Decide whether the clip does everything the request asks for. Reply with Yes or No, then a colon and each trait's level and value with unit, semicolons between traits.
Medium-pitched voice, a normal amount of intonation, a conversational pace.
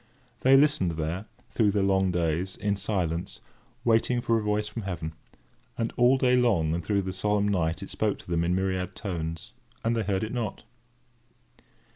No: low, 100 Hz; average, 4.5 semitones; average, 180 wpm